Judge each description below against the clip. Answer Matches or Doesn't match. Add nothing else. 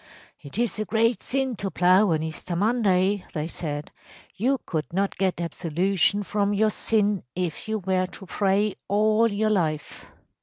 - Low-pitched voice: Doesn't match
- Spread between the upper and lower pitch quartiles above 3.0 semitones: Matches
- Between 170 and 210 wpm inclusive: Doesn't match